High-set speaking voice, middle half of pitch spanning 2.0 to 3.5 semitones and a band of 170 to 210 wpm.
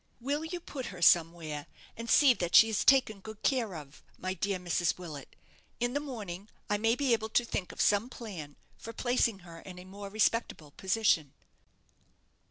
No: high, 205 Hz; average, 5.2 semitones; average, 180 wpm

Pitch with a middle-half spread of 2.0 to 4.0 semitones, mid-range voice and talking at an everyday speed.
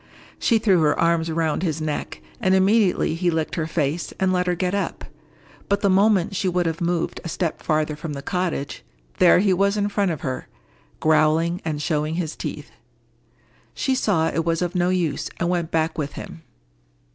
Yes: average, 2.9 semitones; medium, 170 Hz; average, 190 wpm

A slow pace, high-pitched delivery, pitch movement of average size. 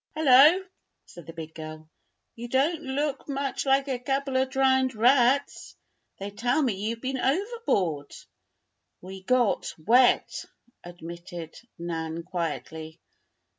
No: slow, 120 wpm; high, 245 Hz; wide, 7.9 semitones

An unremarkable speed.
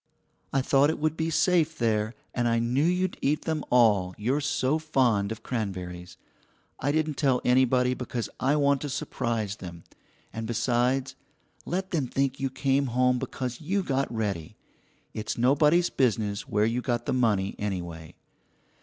Yes: average, 160 wpm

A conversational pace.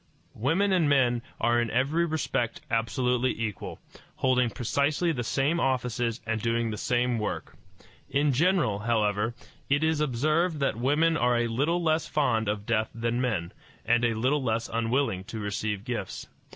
Yes: average, 160 wpm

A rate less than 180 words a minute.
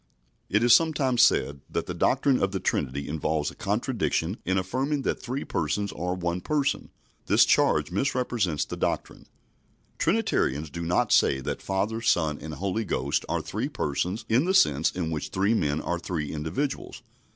Yes: average, 170 wpm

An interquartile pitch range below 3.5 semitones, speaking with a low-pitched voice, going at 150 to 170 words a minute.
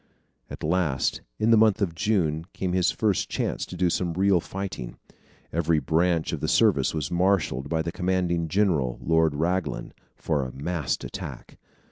Yes: average, 3.0 semitones; very low, 85 Hz; average, 165 wpm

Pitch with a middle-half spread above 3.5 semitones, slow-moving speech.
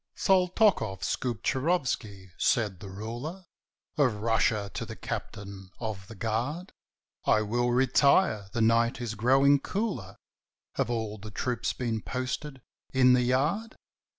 Yes: average, 4.1 semitones; slow, 130 wpm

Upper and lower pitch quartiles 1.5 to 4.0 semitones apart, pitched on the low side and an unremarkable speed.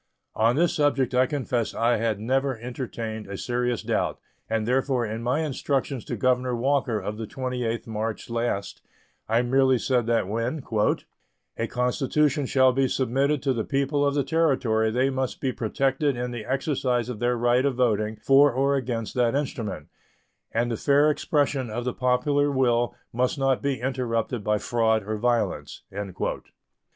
Yes: average, 2.8 semitones; low, 125 Hz; average, 165 wpm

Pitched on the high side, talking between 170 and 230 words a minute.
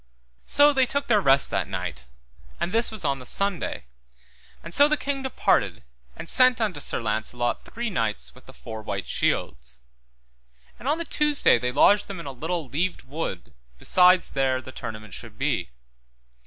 No: medium, 165 Hz; average, 175 wpm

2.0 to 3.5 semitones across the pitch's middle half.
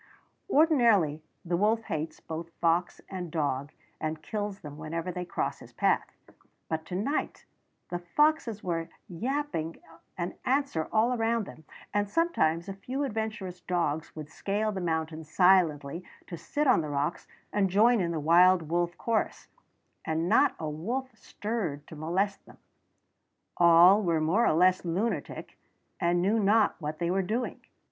No: average, 5.0 semitones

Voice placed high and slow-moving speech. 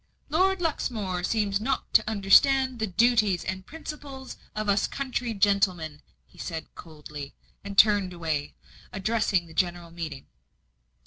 Yes: high, 200 Hz; slow, 130 wpm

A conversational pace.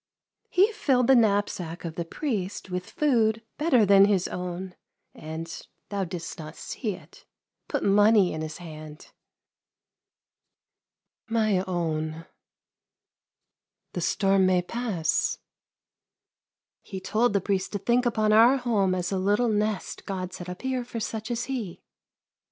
Yes: average, 150 wpm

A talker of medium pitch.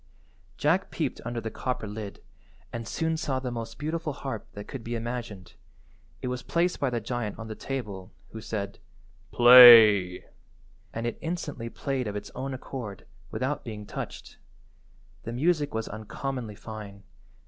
No: low, 120 Hz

